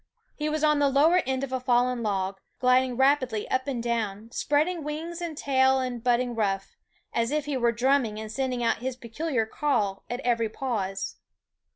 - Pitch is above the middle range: Yes, very high, 255 Hz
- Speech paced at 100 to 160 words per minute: No, average, 195 wpm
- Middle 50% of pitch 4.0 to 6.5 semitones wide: No, average, 3.5 semitones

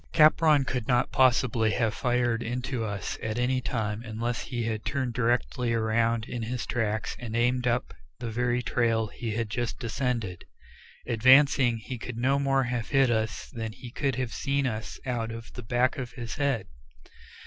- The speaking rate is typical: Yes, average, 175 wpm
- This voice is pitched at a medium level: No, low, 120 Hz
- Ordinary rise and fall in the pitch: No, narrow, 2.0 semitones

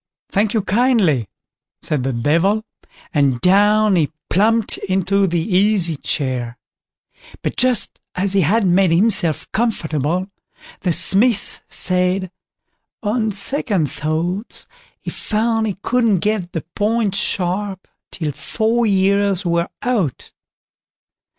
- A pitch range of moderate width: Yes, average, 4.1 semitones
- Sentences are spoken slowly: Yes, slow, 115 wpm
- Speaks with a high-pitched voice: Yes, high, 195 Hz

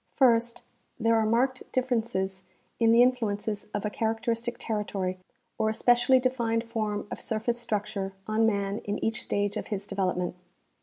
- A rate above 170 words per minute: No, average, 155 wpm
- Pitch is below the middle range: No, high, 225 Hz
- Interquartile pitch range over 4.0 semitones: No, narrow, 2.5 semitones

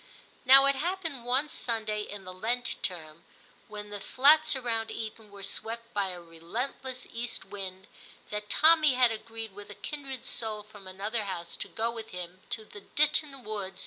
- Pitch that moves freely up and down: No, average, 4.2 semitones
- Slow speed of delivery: No, average, 185 wpm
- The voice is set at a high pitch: Yes, high, 220 Hz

